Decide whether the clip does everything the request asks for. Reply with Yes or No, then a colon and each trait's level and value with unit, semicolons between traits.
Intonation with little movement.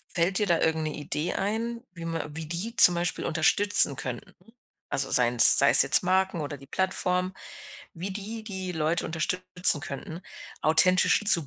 No: average, 3.3 semitones